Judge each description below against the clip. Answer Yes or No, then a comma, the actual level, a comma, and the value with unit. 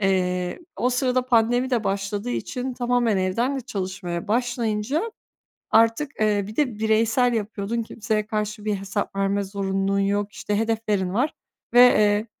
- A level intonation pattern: No, average, 3.4 semitones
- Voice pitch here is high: Yes, high, 215 Hz